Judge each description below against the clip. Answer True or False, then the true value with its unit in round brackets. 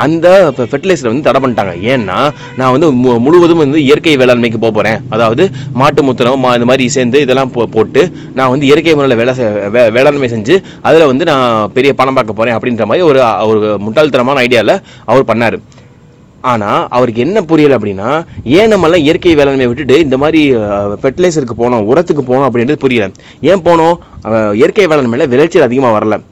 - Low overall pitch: True (130 Hz)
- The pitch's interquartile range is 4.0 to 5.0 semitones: True (4.6 semitones)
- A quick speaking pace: True (160 wpm)